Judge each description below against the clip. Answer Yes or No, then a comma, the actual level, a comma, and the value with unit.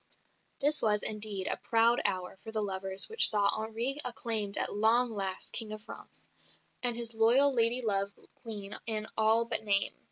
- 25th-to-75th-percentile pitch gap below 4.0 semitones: Yes, narrow, 2.4 semitones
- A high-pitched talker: Yes, high, 220 Hz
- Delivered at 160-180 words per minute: Yes, average, 170 wpm